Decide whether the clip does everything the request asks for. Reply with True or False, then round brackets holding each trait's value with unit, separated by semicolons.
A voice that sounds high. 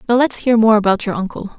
True (220 Hz)